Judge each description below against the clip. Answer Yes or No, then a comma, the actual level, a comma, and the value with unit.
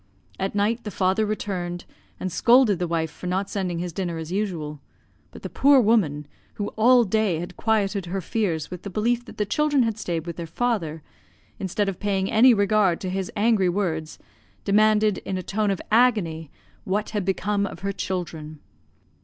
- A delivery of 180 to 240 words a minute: Yes, average, 185 wpm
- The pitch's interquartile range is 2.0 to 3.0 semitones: No, average, 3.6 semitones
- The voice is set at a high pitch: Yes, high, 195 Hz